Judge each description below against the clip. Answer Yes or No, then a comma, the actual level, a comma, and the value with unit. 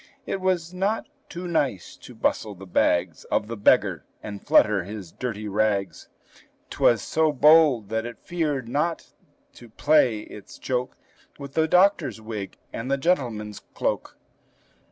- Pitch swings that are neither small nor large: No, wide, 7.1 semitones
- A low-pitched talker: Yes, low, 120 Hz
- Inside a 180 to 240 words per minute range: No, average, 150 wpm